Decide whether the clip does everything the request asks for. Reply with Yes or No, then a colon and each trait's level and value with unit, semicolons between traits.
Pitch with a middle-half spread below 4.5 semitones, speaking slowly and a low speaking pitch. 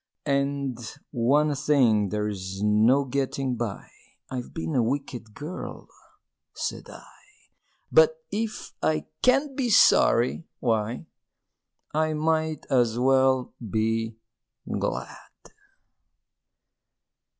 No: average, 5.1 semitones; slow, 95 wpm; low, 130 Hz